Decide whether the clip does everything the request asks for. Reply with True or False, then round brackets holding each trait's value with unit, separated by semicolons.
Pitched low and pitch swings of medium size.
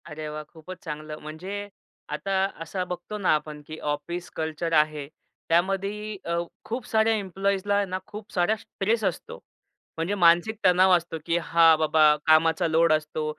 False (170 Hz; 4.0 semitones)